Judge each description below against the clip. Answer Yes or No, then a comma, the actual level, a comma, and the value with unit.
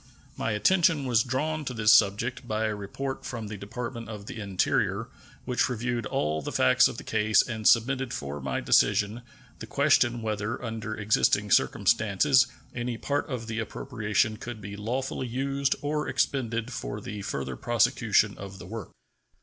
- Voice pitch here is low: Yes, low, 115 Hz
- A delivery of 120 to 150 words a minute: No, average, 165 wpm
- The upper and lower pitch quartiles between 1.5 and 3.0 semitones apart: No, average, 3.5 semitones